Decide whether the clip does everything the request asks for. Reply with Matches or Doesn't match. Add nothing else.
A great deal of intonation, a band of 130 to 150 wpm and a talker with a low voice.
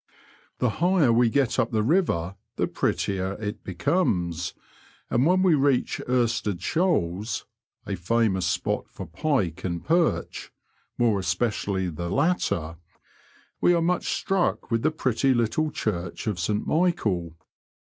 Matches